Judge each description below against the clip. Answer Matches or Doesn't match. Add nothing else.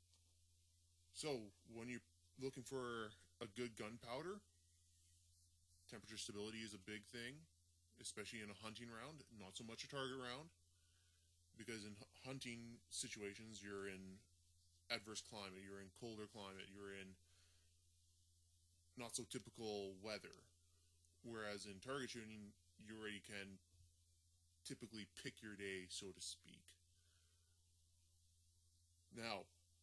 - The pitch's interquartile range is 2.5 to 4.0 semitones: Doesn't match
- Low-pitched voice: Matches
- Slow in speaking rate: Matches